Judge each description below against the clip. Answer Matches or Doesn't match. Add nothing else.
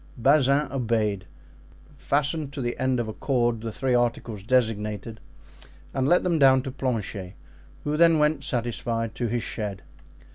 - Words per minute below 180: Matches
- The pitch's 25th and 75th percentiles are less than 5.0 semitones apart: Matches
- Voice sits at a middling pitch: Doesn't match